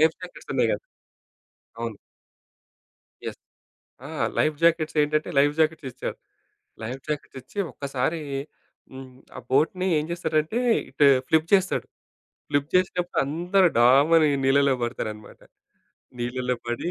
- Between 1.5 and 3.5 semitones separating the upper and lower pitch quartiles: No, average, 3.9 semitones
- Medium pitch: Yes, medium, 150 Hz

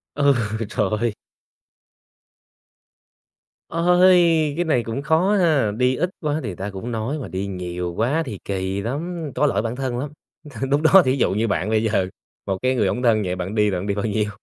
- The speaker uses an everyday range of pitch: No, wide, 6.6 semitones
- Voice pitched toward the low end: Yes, low, 120 Hz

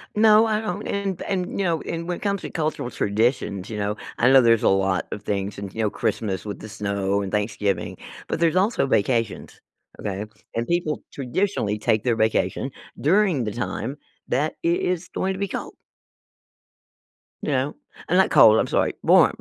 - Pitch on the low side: Yes, low, 125 Hz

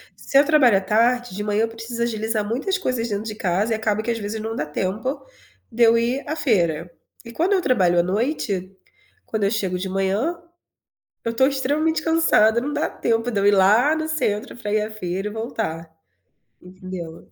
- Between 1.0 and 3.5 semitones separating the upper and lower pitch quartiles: No, average, 4.1 semitones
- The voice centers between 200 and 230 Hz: Yes, high, 220 Hz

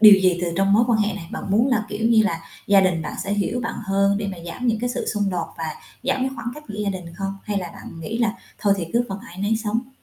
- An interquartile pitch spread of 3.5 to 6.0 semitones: No, average, 3.1 semitones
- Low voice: No, high, 205 Hz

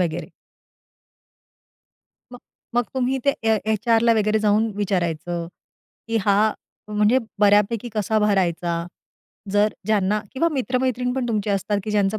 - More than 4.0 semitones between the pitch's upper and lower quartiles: No, average, 2.9 semitones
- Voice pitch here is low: No, high, 210 Hz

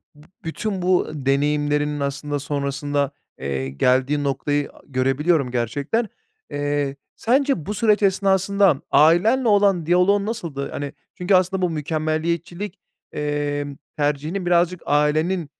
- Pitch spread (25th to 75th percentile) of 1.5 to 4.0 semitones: No, average, 4.4 semitones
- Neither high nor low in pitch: Yes, medium, 150 Hz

